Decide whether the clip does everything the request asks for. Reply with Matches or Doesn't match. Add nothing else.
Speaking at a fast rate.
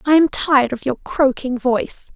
Doesn't match